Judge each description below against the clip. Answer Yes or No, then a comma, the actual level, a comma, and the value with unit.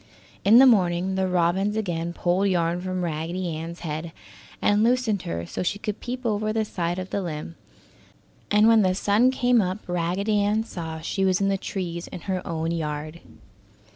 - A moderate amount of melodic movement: Yes, average, 3.5 semitones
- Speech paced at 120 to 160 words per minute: No, average, 185 wpm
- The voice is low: No, medium, 185 Hz